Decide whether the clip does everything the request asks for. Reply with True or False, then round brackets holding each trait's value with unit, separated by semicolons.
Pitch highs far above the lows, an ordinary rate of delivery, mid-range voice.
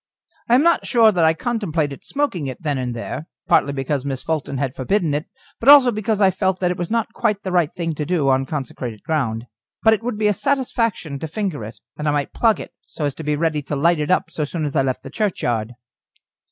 False (6.9 semitones; 240 wpm; 160 Hz)